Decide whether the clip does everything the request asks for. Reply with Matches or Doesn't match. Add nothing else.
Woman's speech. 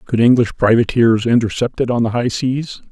Doesn't match